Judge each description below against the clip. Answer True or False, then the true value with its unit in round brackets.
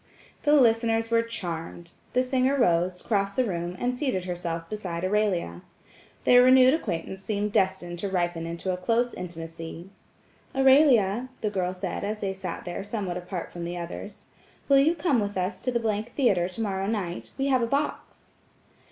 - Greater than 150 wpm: True (170 wpm)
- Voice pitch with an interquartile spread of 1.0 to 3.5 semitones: False (5.2 semitones)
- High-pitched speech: True (200 Hz)